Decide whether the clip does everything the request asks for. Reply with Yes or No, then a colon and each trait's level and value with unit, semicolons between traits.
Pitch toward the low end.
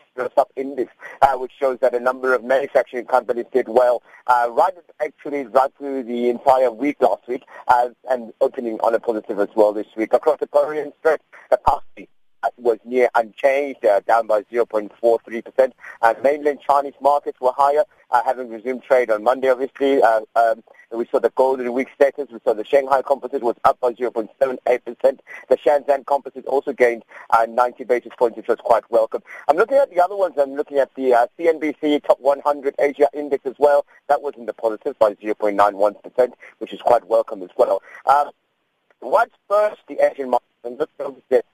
Yes: low, 130 Hz